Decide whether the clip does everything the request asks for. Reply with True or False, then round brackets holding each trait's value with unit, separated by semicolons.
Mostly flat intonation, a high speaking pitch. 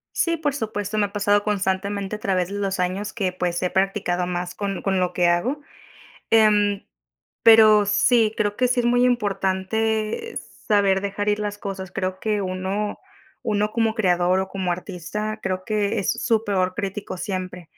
True (2.3 semitones; 200 Hz)